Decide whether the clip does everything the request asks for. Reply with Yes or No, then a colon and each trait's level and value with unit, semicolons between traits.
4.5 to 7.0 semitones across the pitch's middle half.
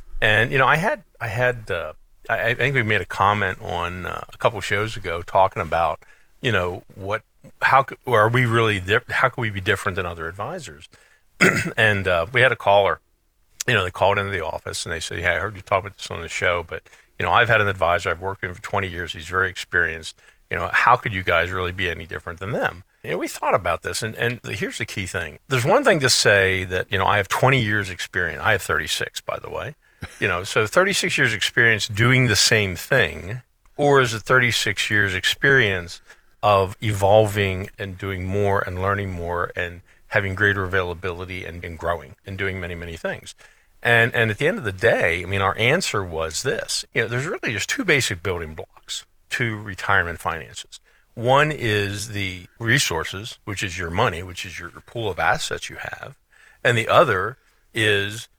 No: average, 3.8 semitones